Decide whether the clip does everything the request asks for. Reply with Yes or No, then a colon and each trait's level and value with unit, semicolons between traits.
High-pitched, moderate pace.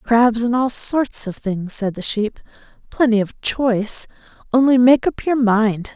Yes: high, 230 Hz; average, 170 wpm